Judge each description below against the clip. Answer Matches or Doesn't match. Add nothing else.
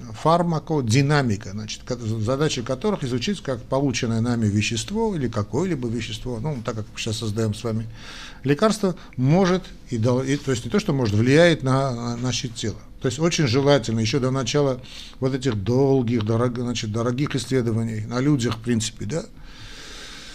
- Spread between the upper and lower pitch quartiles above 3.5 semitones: Matches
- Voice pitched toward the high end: Doesn't match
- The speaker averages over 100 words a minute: Matches